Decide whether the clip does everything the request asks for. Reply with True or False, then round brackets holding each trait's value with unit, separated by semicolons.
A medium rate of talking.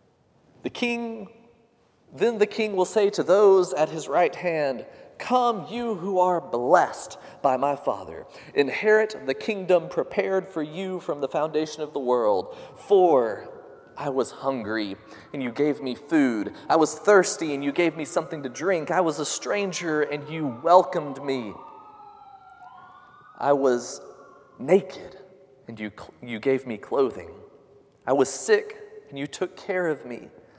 True (155 wpm)